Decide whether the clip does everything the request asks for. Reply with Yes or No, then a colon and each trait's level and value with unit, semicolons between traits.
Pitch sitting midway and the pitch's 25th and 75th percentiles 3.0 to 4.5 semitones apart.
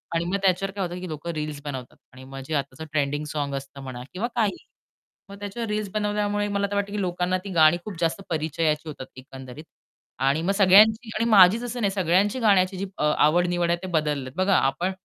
No: medium, 175 Hz; average, 5.0 semitones